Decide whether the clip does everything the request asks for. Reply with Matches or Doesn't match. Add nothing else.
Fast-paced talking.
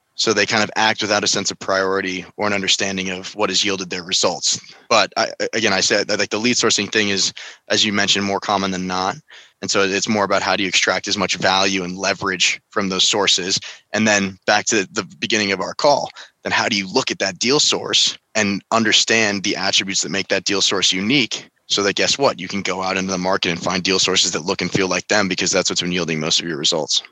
Matches